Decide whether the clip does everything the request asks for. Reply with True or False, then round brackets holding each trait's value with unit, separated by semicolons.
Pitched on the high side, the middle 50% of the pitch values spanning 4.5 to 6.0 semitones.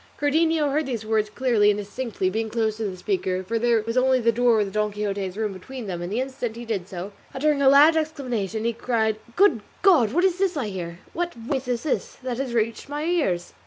True (230 Hz; 4.8 semitones)